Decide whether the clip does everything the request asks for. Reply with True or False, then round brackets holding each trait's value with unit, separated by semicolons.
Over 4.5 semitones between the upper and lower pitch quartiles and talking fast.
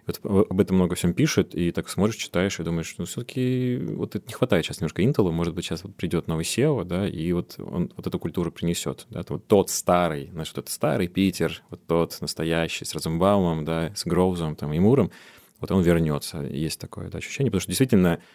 False (3.6 semitones; 220 wpm)